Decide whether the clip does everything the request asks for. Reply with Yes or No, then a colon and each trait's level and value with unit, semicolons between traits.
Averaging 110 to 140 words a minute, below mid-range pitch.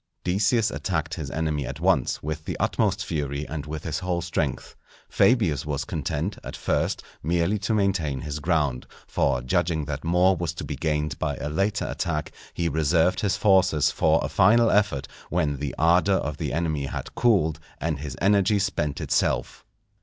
No: average, 175 wpm; very low, 80 Hz